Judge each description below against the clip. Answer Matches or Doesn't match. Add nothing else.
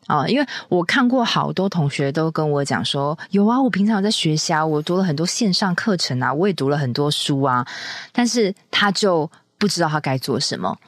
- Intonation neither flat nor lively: Doesn't match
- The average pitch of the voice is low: Doesn't match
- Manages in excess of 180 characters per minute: Matches